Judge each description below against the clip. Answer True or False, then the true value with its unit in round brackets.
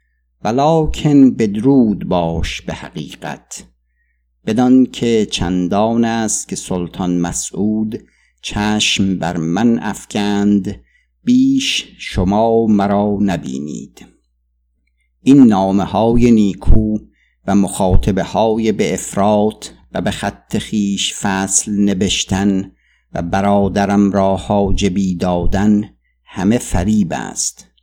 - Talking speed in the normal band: False (90 wpm)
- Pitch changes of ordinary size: True (3.5 semitones)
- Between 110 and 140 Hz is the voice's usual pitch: False (100 Hz)